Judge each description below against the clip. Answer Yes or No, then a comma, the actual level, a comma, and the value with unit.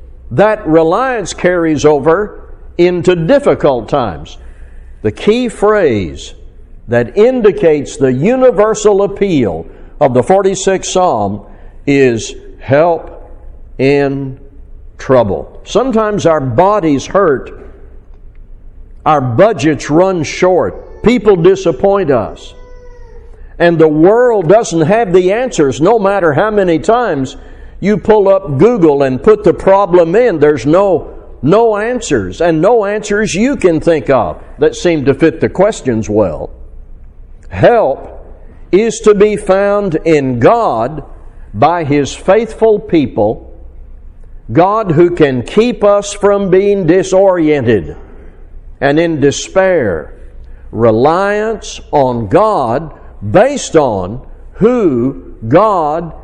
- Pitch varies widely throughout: Yes, wide, 7.0 semitones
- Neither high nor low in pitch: Yes, medium, 175 Hz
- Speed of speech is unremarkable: No, slow, 110 wpm